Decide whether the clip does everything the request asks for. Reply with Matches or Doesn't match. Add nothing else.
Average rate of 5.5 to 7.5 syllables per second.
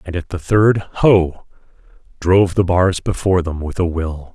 Doesn't match